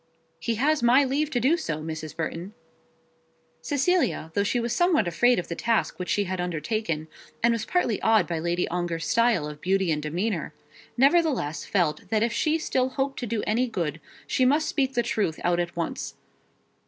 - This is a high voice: Yes, high, 215 Hz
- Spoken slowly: No, average, 190 wpm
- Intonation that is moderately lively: No, wide, 7.2 semitones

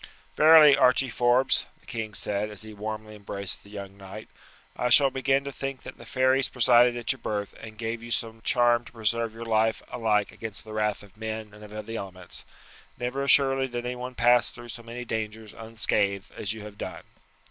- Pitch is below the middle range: Yes, low, 115 Hz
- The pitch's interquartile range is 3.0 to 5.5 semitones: No, narrow, 2.5 semitones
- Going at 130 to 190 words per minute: No, average, 200 wpm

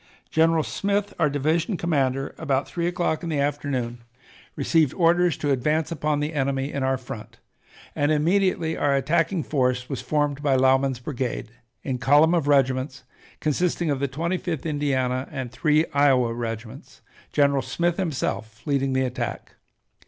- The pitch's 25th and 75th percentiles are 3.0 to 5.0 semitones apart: Yes, average, 3.5 semitones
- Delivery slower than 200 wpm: Yes, average, 150 wpm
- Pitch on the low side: No, medium, 145 Hz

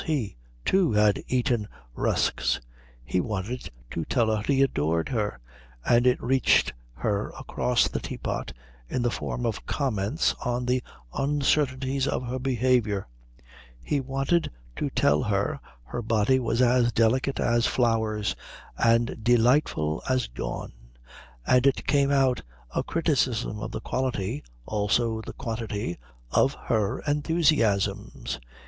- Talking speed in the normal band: No, slow, 130 wpm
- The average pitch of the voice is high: No, low, 120 Hz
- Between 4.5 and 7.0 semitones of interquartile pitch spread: No, average, 3.9 semitones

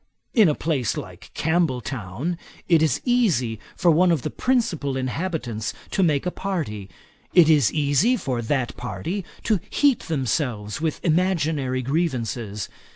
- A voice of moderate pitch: Yes, medium, 150 Hz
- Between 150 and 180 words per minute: No, average, 140 wpm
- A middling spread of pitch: No, wide, 5.9 semitones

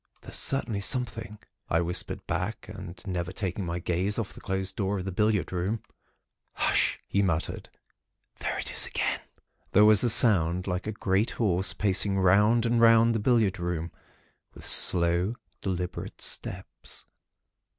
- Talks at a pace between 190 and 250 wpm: No, average, 150 wpm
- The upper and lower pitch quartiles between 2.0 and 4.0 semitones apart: Yes, average, 3.2 semitones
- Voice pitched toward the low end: Yes, very low, 95 Hz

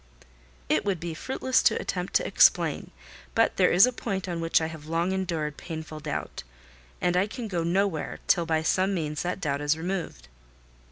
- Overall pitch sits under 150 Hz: No, medium, 170 Hz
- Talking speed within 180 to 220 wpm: Yes, average, 185 wpm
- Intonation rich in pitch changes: No, average, 3.2 semitones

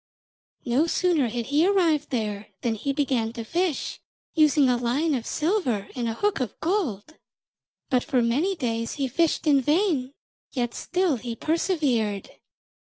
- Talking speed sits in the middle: Yes, average, 155 wpm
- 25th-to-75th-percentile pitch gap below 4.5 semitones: No, wide, 5.6 semitones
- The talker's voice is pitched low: No, very high, 275 Hz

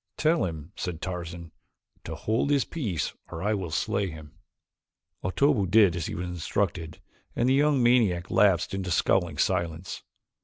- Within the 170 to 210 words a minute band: No, average, 155 wpm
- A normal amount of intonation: Yes, average, 4.7 semitones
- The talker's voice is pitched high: No, very low, 90 Hz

